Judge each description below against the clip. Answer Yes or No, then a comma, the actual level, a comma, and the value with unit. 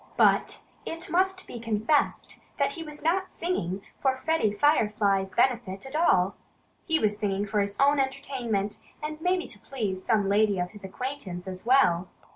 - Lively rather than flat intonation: Yes, wide, 6.7 semitones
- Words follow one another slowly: No, average, 165 wpm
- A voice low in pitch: No, high, 230 Hz